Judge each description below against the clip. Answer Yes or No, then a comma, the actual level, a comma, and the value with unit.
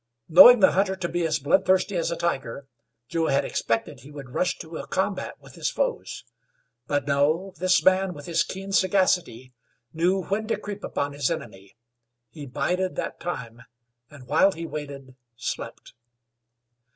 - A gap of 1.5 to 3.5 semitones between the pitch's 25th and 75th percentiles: No, average, 5.0 semitones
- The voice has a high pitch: No, medium, 165 Hz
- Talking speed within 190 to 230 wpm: No, average, 165 wpm